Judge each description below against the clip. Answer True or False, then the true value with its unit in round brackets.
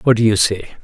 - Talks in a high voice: False (110 Hz)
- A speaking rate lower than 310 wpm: True (285 wpm)